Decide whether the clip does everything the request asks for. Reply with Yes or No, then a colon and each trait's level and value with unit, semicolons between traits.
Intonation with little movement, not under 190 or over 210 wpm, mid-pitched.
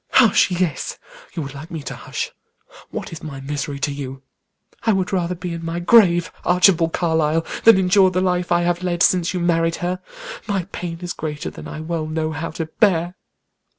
Yes: narrow, 2.3 semitones; average, 195 wpm; medium, 170 Hz